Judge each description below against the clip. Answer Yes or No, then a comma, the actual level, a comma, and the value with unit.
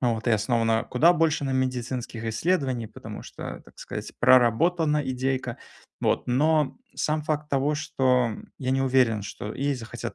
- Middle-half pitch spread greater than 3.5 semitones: Yes, average, 4.0 semitones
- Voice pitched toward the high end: No, low, 130 Hz